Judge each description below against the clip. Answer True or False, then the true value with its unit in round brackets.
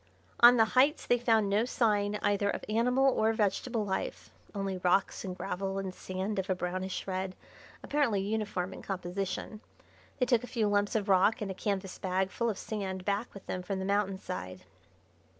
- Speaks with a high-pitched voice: True (200 Hz)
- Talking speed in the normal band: True (185 wpm)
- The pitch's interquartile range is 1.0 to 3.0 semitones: True (2.6 semitones)